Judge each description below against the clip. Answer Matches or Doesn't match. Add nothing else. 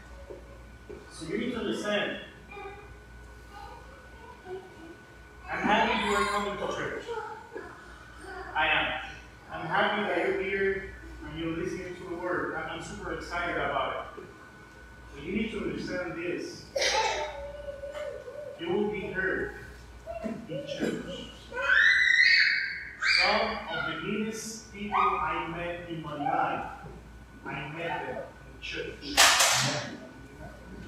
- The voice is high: Matches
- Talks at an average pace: Doesn't match